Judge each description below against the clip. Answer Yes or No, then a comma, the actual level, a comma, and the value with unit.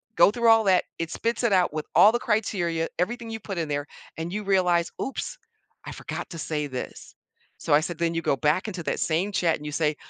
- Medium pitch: Yes, medium, 175 Hz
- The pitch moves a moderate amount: Yes, average, 4.6 semitones